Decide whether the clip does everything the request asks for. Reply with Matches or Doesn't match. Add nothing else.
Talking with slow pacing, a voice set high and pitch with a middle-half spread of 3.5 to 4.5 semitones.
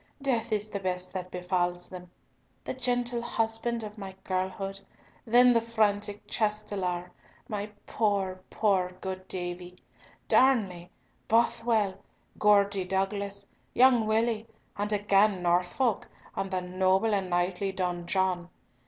Doesn't match